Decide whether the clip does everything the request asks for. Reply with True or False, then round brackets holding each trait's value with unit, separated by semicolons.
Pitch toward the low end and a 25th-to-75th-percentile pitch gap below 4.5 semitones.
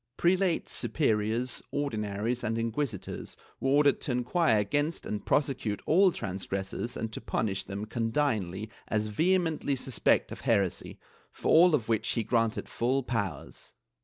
False (115 Hz; 5.3 semitones)